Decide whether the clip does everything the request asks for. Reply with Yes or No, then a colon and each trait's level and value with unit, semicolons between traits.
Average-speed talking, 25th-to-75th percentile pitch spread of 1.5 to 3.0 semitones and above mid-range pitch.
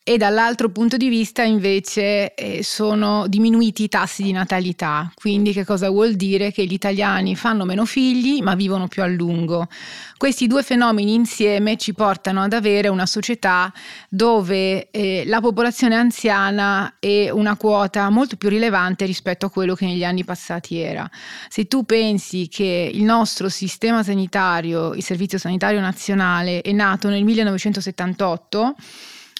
Yes: average, 150 wpm; average, 2.7 semitones; high, 200 Hz